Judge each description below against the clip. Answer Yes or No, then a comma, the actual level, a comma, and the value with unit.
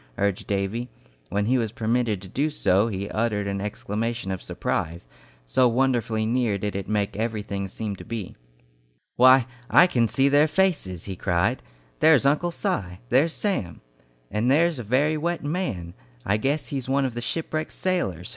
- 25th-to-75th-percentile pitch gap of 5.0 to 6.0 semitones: Yes, wide, 5.6 semitones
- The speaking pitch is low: Yes, low, 115 Hz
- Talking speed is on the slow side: No, average, 170 wpm